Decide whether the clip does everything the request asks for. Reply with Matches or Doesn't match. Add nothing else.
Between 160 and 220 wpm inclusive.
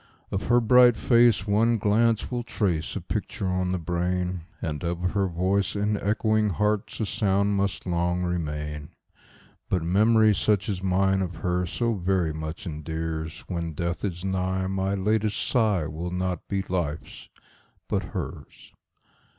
Doesn't match